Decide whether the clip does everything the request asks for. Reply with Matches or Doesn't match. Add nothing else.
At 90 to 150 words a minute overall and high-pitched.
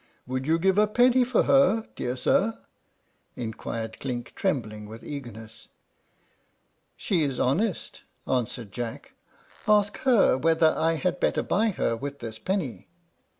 Doesn't match